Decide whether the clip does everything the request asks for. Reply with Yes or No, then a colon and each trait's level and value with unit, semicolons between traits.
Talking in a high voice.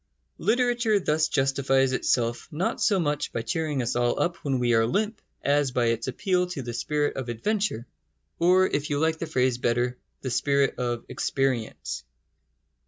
No: low, 135 Hz